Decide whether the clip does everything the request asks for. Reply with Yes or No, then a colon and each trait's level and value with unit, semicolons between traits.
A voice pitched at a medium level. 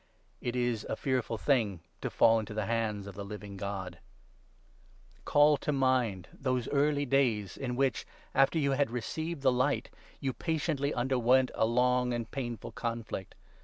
No: low, 125 Hz